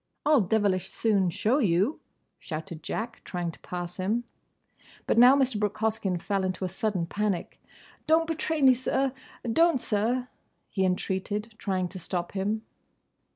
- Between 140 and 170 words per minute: Yes, average, 150 wpm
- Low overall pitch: No, high, 205 Hz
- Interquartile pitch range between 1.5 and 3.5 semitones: No, average, 4.5 semitones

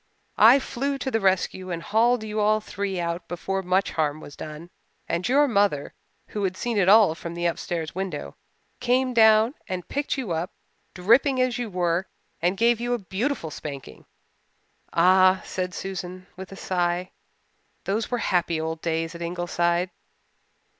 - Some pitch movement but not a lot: Yes, average, 4.4 semitones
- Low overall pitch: No, medium, 185 Hz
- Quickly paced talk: No, average, 165 wpm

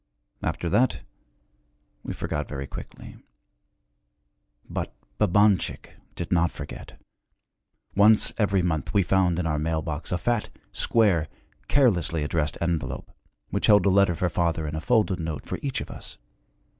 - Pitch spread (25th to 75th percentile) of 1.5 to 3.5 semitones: No, average, 4.1 semitones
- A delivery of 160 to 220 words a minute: No, average, 145 wpm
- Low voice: Yes, very low, 85 Hz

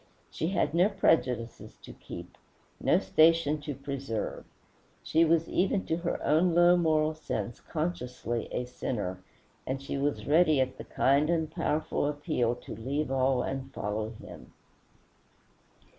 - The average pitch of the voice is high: No, medium, 145 Hz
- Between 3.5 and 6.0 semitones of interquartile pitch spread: Yes, average, 4.5 semitones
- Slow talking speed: No, average, 145 wpm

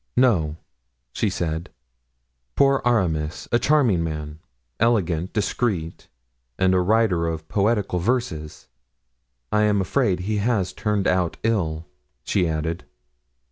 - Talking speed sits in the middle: No, slow, 115 wpm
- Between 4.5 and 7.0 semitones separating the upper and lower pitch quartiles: Yes, wide, 5.5 semitones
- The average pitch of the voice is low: Yes, very low, 95 Hz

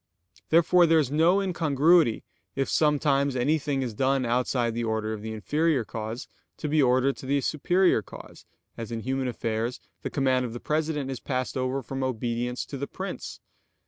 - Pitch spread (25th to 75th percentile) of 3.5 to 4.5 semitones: Yes, average, 3.9 semitones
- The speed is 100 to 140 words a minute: No, average, 175 wpm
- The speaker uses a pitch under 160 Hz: Yes, low, 135 Hz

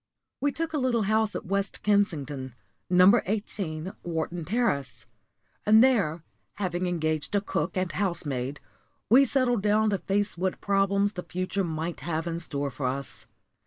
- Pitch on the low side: No, medium, 185 Hz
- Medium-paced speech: Yes, average, 155 wpm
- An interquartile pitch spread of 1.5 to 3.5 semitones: No, average, 4.8 semitones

